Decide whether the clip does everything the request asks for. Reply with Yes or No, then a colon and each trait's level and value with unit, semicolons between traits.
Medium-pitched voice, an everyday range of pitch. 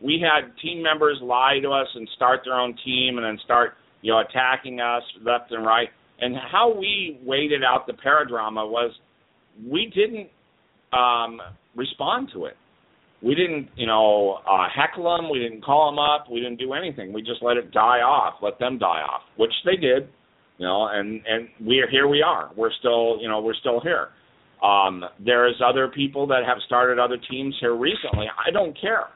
No: low, 125 Hz; average, 3.8 semitones